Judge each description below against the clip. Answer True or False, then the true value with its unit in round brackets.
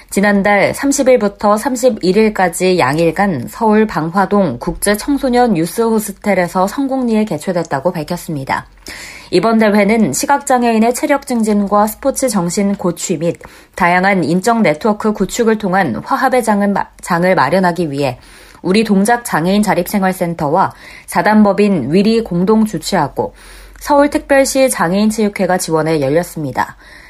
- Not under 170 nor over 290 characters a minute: False (310 characters per minute)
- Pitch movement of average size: True (4.2 semitones)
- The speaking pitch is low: False (200 Hz)